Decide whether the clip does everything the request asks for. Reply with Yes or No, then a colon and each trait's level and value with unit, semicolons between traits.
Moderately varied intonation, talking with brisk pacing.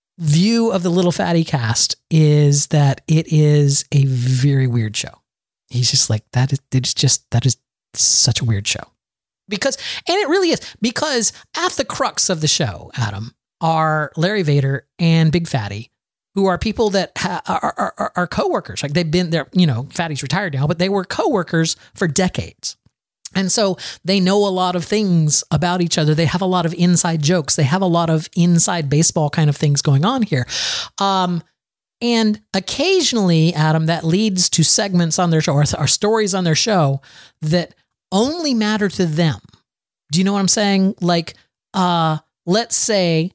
No: average, 5.0 semitones; average, 185 wpm